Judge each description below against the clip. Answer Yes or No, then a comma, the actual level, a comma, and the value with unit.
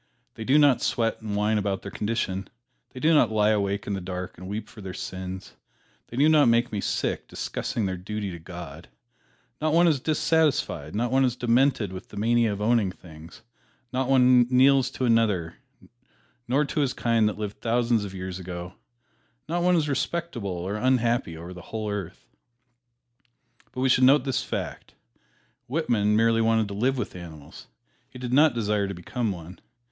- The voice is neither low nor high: No, low, 110 Hz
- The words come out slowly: No, average, 185 wpm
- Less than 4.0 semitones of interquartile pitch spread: No, average, 4.8 semitones